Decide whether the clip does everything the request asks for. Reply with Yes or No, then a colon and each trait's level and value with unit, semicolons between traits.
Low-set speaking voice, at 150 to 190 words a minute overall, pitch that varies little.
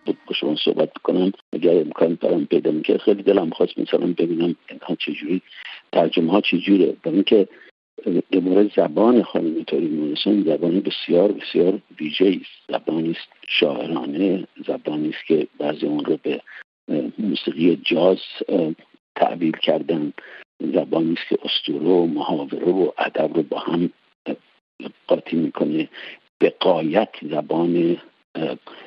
No: very low, 85 Hz; average, 130 wpm; narrow, 1.5 semitones